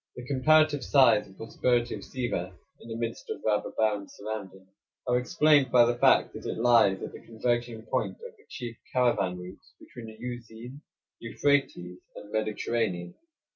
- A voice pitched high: No, low, 115 Hz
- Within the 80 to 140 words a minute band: No, average, 165 wpm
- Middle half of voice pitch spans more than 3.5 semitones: No, average, 3.1 semitones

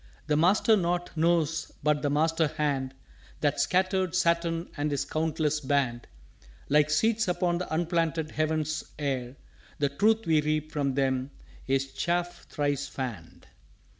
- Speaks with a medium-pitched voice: Yes, medium, 155 Hz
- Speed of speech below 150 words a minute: Yes, average, 140 wpm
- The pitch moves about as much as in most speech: Yes, average, 3.1 semitones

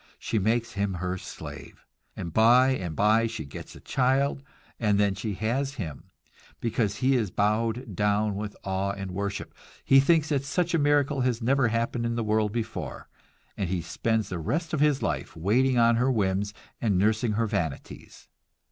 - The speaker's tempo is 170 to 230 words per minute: Yes, average, 180 wpm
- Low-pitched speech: Yes, low, 110 Hz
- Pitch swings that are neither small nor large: Yes, average, 4.2 semitones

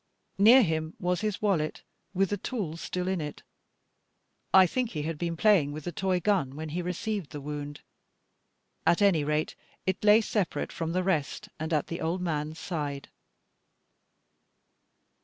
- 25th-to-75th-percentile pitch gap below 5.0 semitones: Yes, average, 3.9 semitones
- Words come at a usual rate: Yes, average, 160 wpm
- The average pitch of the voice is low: No, medium, 170 Hz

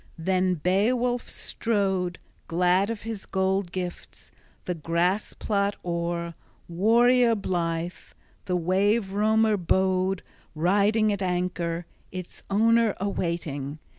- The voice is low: No, high, 190 Hz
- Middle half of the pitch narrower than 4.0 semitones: Yes, average, 3.0 semitones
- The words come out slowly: Yes, slow, 105 wpm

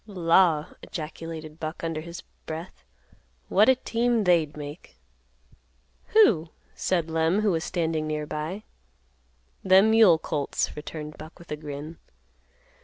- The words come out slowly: Yes, slow, 125 wpm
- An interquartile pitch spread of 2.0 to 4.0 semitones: Yes, average, 3.3 semitones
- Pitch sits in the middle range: Yes, medium, 165 Hz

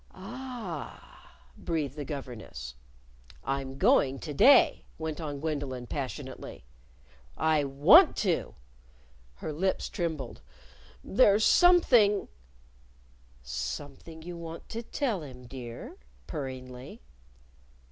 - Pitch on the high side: No, medium, 145 Hz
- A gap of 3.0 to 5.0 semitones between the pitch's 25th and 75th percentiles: No, wide, 5.5 semitones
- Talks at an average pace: No, slow, 95 wpm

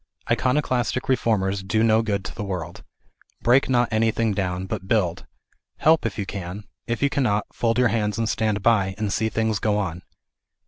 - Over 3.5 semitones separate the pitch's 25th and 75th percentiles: No, average, 2.8 semitones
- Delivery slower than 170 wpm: No, average, 180 wpm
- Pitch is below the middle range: Yes, low, 110 Hz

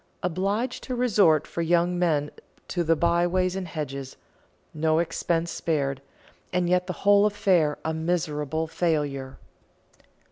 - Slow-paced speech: Yes, slow, 130 wpm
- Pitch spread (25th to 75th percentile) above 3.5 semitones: No, average, 2.7 semitones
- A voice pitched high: No, medium, 170 Hz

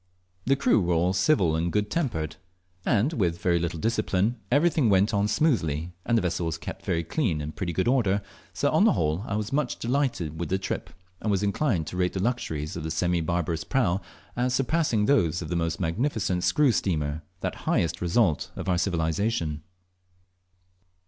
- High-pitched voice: No, very low, 95 Hz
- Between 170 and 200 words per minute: Yes, average, 195 wpm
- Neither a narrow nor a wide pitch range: No, wide, 5.8 semitones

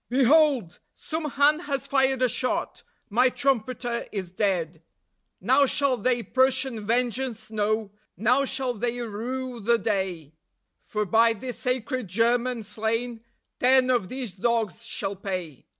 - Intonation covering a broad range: No, average, 3.5 semitones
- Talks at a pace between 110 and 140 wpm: Yes, slow, 135 wpm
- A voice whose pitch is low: No, high, 235 Hz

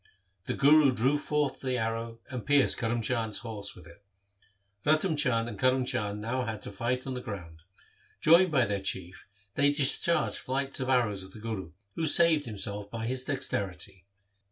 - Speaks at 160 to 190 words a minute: Yes, average, 180 wpm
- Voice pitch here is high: No, low, 120 Hz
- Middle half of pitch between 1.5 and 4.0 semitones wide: No, average, 4.9 semitones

